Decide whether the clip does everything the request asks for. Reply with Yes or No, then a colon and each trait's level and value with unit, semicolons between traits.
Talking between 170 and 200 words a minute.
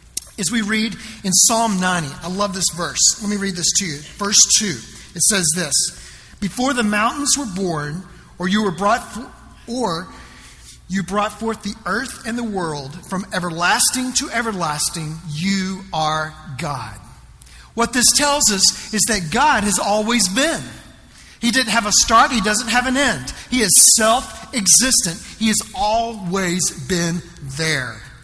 No: average, 160 wpm